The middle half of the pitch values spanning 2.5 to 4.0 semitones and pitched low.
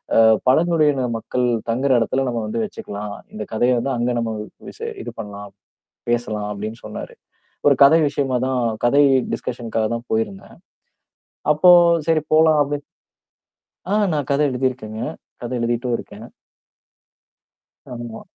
No: average, 4.4 semitones; low, 125 Hz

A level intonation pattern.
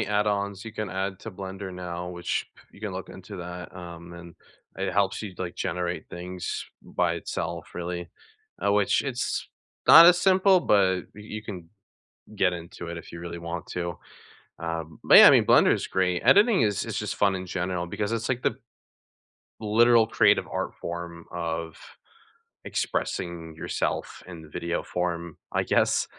No: average, 3.0 semitones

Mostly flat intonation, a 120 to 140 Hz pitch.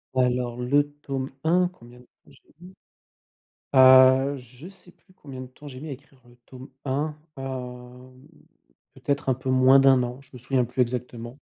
Yes: narrow, 2.0 semitones; low, 130 Hz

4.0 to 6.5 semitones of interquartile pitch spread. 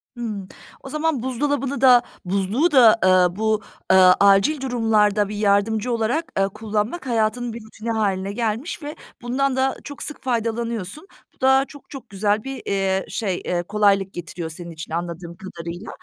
Yes: average, 4.9 semitones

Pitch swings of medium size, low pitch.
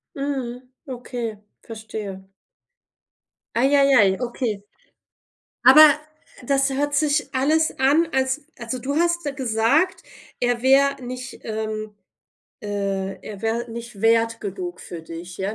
No: average, 4.3 semitones; high, 240 Hz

